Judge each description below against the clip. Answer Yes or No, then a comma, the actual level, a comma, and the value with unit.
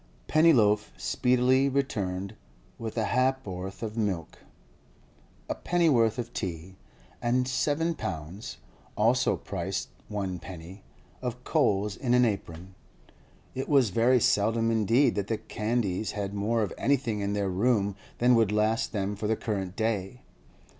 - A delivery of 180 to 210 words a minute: No, slow, 135 wpm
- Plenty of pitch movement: No, average, 4.0 semitones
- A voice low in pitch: Yes, low, 110 Hz